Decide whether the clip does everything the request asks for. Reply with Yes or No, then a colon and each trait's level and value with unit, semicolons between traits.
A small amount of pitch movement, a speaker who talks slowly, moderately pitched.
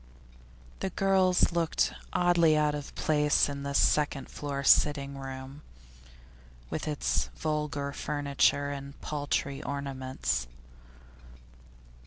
Yes: narrow, 1.6 semitones; slow, 100 wpm; medium, 145 Hz